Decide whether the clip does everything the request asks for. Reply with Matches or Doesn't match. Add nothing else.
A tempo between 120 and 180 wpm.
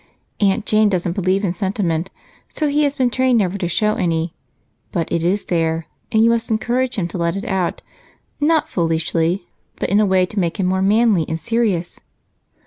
Doesn't match